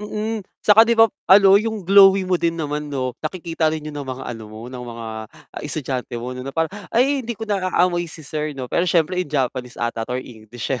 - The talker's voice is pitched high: No, medium, 155 Hz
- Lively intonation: Yes, wide, 7.2 semitones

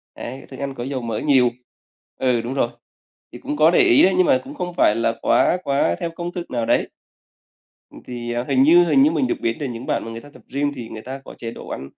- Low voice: Yes, low, 130 Hz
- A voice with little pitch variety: No, average, 3.9 semitones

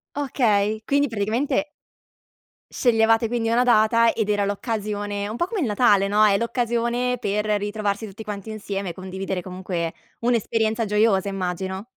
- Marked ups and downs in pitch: No, average, 2.7 semitones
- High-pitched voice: Yes, high, 215 Hz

